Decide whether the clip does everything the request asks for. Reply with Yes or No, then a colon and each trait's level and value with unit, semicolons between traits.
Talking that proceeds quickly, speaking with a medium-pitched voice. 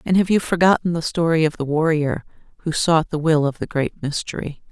Yes: fast, 215 wpm; medium, 160 Hz